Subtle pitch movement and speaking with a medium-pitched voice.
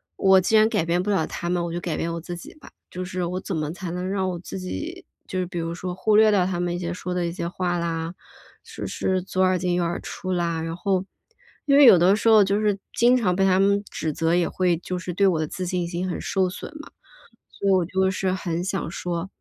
Yes: narrow, 1.9 semitones; medium, 180 Hz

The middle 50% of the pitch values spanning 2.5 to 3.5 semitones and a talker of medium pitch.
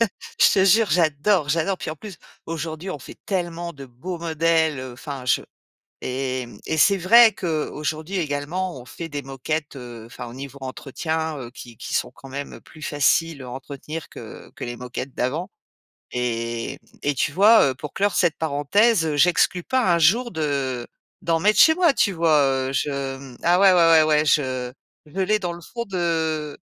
No: average, 4.6 semitones; medium, 155 Hz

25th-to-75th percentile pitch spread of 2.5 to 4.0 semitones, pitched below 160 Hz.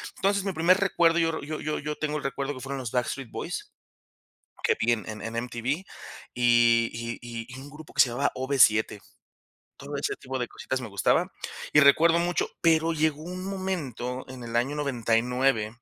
No: average, 4.8 semitones; low, 135 Hz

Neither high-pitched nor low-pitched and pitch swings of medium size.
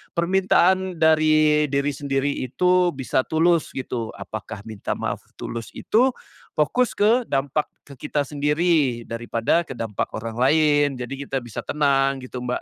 Yes: medium, 145 Hz; average, 4.2 semitones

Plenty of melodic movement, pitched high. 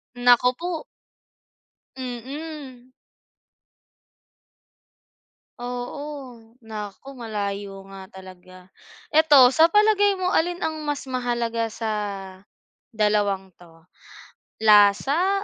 Yes: wide, 6.4 semitones; high, 245 Hz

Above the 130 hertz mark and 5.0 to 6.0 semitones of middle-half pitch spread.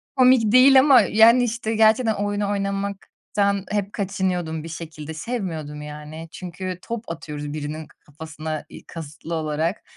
Yes: medium, 185 Hz; wide, 5.5 semitones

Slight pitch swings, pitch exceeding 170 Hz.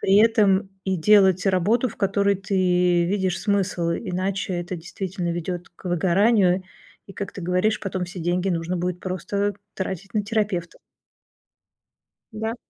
Yes: narrow, 2.1 semitones; high, 190 Hz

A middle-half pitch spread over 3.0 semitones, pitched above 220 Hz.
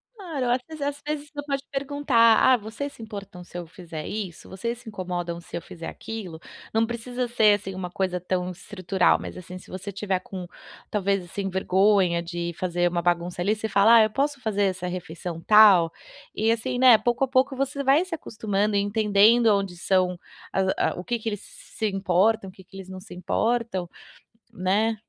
No: average, 4.4 semitones; high, 200 Hz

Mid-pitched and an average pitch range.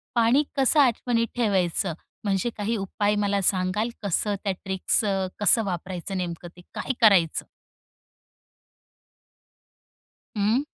No: high, 205 Hz; average, 3.5 semitones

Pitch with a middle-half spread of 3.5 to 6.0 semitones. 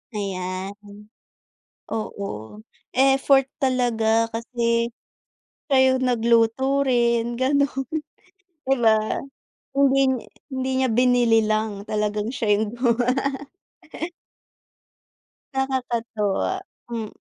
No: average, 3.1 semitones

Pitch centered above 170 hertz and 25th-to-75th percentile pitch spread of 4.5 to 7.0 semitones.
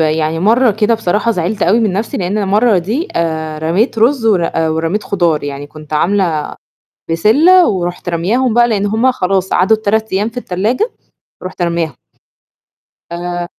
Yes: high, 190 Hz; average, 4.8 semitones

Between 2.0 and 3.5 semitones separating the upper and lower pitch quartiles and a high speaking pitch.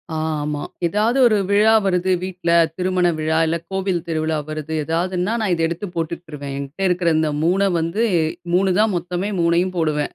No: average, 2.9 semitones; medium, 175 Hz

